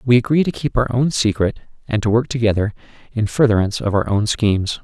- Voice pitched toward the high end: No, low, 115 Hz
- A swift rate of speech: Yes, fast, 210 wpm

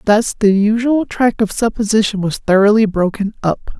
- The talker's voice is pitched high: Yes, high, 210 Hz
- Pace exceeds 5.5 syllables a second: No, 5.1 syllables/s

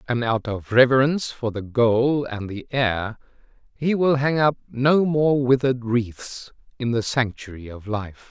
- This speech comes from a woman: No, male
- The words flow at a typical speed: Yes, average, 165 wpm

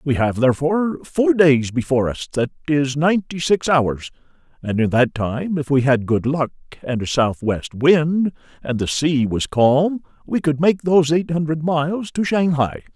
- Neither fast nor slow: Yes, average, 180 wpm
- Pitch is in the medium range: Yes, medium, 145 Hz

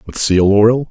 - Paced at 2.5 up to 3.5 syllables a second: No, 3.9 syllables/s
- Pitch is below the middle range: Yes, low, 110 Hz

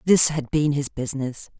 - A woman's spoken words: Yes, female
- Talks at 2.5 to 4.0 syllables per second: No, 5.2 syllables/s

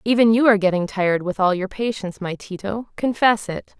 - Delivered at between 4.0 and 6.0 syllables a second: Yes, 5.8 syllables/s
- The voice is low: No, high, 205 Hz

